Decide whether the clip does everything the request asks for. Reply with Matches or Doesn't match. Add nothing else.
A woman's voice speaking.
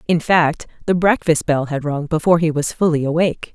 Matches